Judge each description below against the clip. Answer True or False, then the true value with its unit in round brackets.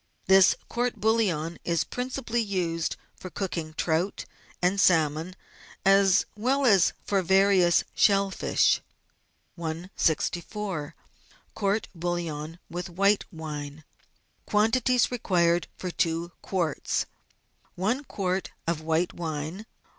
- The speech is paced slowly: True (100 wpm)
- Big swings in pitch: False (3.4 semitones)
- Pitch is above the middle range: False (180 Hz)